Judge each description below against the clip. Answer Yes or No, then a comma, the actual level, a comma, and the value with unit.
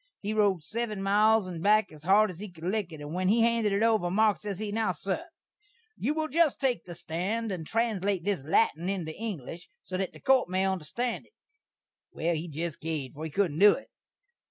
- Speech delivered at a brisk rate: Yes, fast, 215 wpm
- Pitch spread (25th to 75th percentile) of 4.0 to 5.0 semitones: Yes, average, 4.3 semitones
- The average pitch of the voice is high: Yes, high, 195 Hz